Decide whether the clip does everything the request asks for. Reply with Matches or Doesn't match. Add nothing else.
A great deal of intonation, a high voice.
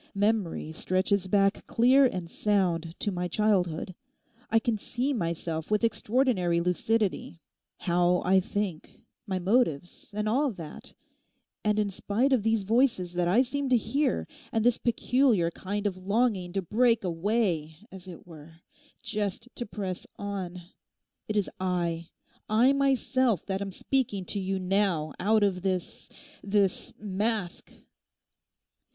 Doesn't match